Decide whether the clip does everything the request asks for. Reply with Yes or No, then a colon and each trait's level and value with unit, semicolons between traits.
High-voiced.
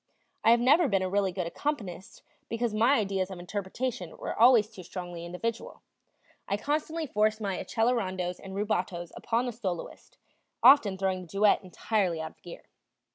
Yes: high, 200 Hz